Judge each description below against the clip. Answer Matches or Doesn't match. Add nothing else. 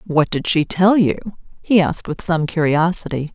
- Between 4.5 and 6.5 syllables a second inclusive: Matches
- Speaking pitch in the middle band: Matches